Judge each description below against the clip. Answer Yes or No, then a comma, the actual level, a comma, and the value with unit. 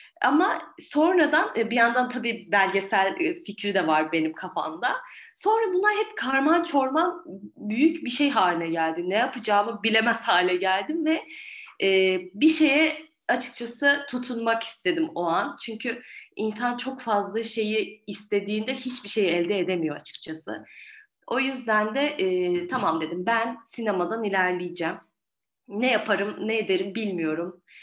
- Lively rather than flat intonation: Yes, wide, 6.1 semitones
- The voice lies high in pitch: Yes, high, 225 Hz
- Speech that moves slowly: No, average, 125 wpm